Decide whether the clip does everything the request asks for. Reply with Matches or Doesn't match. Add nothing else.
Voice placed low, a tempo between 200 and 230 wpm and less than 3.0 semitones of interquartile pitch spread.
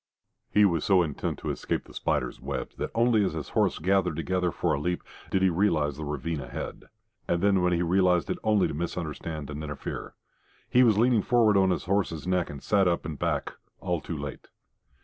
Doesn't match